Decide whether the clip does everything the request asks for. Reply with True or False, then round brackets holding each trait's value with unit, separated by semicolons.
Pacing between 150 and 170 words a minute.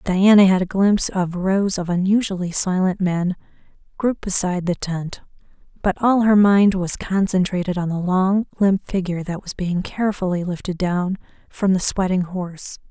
True (165 wpm)